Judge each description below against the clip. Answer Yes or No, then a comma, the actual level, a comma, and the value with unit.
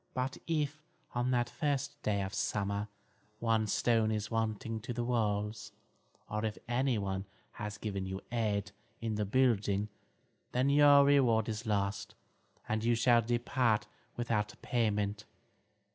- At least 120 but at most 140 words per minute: Yes, slow, 135 wpm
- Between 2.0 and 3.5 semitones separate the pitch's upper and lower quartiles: Yes, average, 2.7 semitones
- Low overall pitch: Yes, low, 110 Hz